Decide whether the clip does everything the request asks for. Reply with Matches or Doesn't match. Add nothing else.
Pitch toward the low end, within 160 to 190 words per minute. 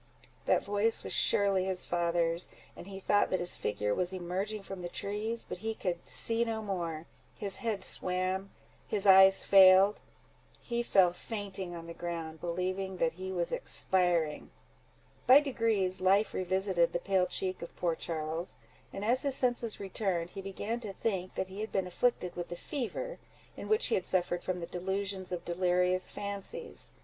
Doesn't match